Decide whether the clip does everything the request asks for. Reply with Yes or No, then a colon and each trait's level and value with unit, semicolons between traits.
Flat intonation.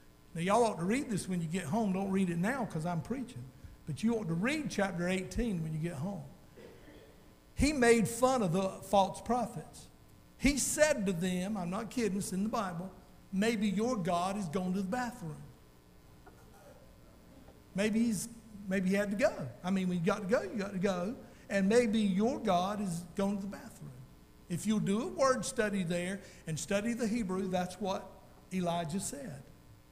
No: average, 3.8 semitones